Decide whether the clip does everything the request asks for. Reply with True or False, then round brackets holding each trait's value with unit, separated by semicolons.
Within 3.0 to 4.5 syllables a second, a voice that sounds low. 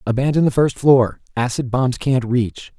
True (4.4 syllables/s; 125 Hz)